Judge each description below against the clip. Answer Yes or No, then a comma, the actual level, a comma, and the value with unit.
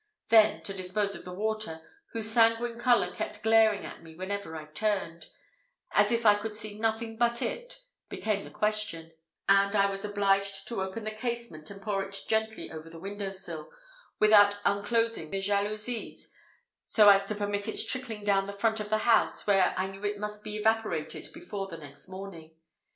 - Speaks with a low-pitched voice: No, high, 205 Hz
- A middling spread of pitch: No, narrow, 2.1 semitones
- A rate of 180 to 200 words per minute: Yes, average, 185 wpm